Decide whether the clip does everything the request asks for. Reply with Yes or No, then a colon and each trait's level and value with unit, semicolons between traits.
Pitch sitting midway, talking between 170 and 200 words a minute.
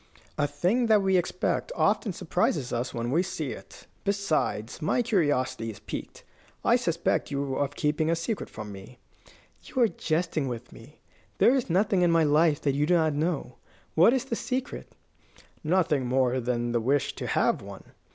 Yes: medium, 155 Hz; average, 180 wpm